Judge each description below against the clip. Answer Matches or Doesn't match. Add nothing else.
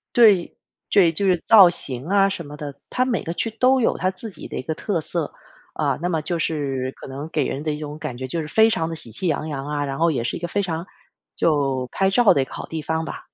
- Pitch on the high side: Doesn't match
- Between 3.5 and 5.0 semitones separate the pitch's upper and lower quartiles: Matches